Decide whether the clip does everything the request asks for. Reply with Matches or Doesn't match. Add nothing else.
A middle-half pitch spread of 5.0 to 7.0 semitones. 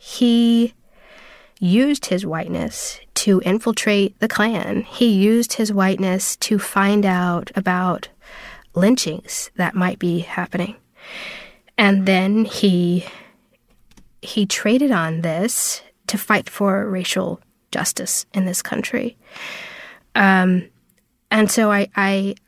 Doesn't match